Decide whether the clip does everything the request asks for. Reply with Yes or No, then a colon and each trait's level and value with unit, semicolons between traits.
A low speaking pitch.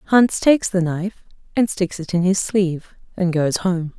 No: medium, 185 Hz